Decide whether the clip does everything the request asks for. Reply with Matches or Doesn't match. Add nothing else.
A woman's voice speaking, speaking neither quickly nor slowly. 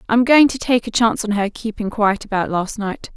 Doesn't match